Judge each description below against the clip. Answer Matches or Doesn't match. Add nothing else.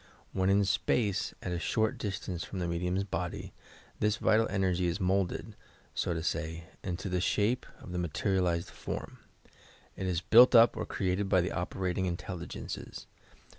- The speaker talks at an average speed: Matches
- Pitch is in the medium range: Doesn't match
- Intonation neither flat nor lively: Doesn't match